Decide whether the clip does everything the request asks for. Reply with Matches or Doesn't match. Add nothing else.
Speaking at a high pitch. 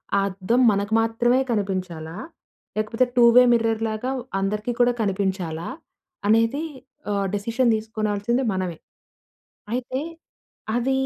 Matches